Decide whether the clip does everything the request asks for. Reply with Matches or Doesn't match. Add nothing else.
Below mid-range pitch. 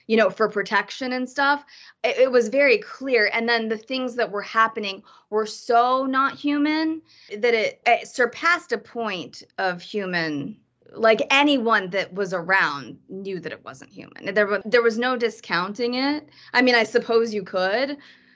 Doesn't match